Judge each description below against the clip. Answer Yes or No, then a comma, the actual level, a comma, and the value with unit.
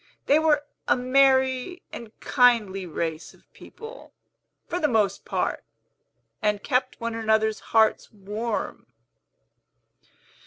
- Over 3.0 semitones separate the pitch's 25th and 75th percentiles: Yes, average, 4.1 semitones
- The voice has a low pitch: No, high, 230 Hz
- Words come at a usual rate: No, slow, 110 wpm